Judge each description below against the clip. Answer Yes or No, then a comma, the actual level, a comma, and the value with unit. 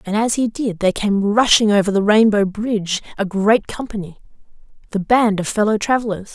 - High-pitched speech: Yes, high, 210 Hz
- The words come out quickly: No, average, 170 wpm